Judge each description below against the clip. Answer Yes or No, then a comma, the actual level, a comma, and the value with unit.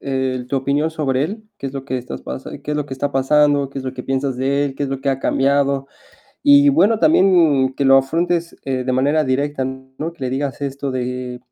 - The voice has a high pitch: No, low, 135 Hz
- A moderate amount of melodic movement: No, narrow, 1.7 semitones